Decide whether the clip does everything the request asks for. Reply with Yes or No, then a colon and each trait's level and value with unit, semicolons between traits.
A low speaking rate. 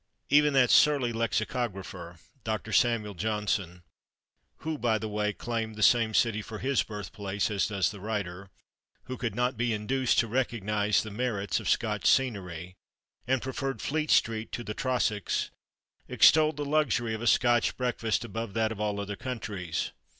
No: average, 160 wpm